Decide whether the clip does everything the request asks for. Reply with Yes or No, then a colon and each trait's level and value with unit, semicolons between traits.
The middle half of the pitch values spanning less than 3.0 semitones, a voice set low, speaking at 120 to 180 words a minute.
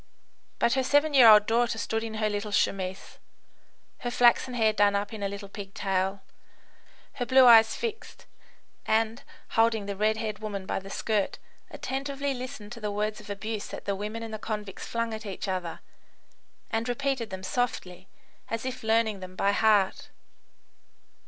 No: narrow, 2.5 semitones; high, 220 Hz; average, 170 wpm